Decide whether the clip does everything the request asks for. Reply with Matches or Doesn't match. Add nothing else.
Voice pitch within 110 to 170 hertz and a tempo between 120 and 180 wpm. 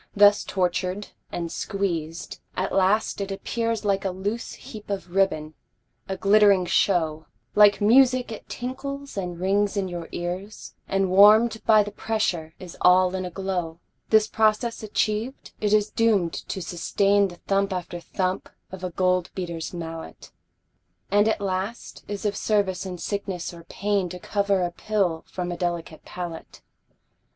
Doesn't match